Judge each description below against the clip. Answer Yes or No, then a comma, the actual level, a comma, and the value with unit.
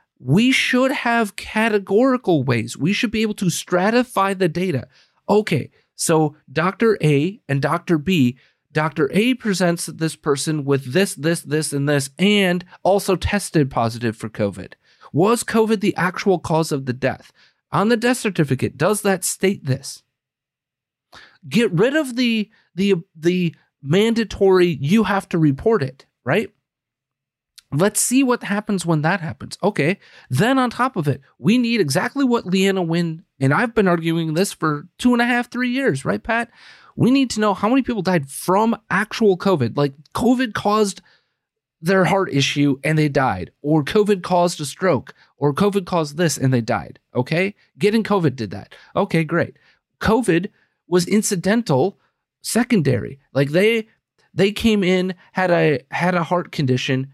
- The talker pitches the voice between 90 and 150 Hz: No, medium, 180 Hz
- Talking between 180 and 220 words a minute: No, average, 160 wpm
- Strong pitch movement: Yes, wide, 6.0 semitones